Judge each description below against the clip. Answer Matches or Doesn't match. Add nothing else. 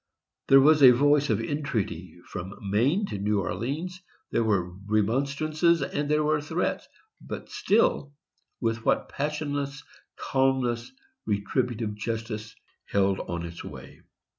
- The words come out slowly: Matches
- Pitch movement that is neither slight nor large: Doesn't match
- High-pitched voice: Doesn't match